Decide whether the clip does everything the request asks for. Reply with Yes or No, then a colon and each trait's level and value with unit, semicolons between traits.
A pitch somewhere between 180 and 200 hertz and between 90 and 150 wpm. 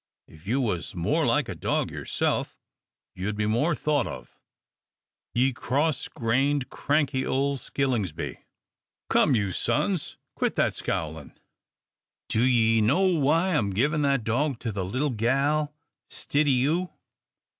No: low, 130 Hz; slow, 135 wpm